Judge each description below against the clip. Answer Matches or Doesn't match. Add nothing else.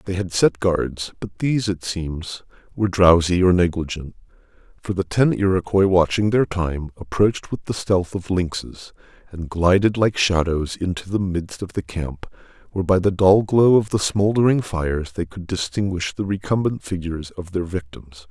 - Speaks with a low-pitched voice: Matches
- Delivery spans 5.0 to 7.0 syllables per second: Doesn't match